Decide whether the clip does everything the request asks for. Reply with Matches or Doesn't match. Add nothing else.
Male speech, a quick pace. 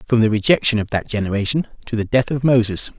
Matches